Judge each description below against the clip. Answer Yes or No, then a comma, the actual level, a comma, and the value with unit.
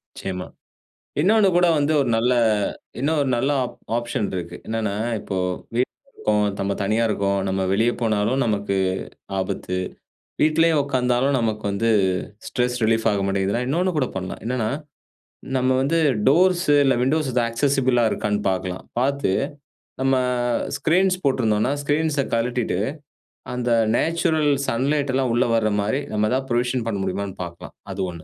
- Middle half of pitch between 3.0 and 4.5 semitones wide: No, average, 5.2 semitones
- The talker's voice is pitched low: Yes, low, 120 Hz